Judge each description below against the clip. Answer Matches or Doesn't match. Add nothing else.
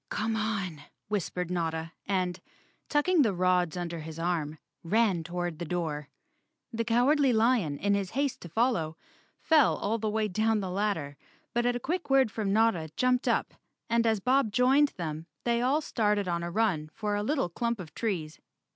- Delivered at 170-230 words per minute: Matches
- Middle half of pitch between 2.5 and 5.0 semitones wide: Doesn't match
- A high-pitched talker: Matches